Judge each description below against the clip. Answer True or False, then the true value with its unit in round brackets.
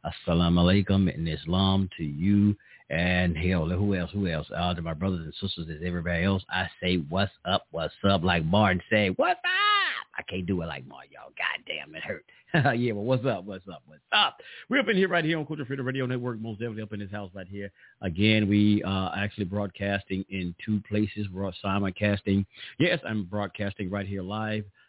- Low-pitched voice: True (100 Hz)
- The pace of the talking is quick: True (210 wpm)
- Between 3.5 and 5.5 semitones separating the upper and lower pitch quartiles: False (2.8 semitones)